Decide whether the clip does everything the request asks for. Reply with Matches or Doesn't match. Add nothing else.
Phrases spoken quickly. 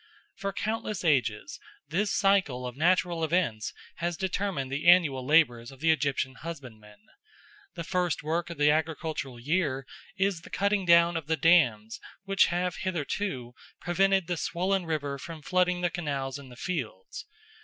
Doesn't match